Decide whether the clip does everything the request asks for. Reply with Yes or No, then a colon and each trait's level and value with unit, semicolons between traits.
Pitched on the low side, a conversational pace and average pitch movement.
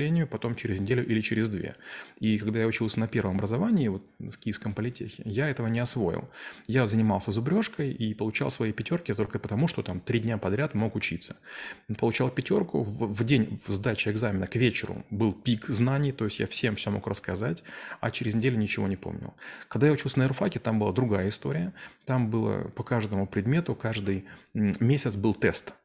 No: low, 115 Hz; fast, 185 wpm; average, 3.3 semitones